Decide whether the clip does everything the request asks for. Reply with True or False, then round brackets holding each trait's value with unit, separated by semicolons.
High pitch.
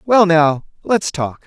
False (165 Hz)